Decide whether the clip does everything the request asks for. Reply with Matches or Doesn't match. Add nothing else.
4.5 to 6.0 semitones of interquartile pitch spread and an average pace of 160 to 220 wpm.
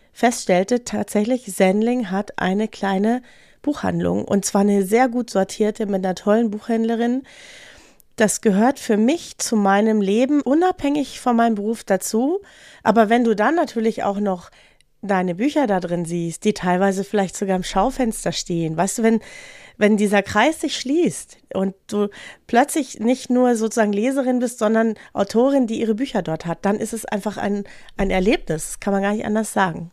Doesn't match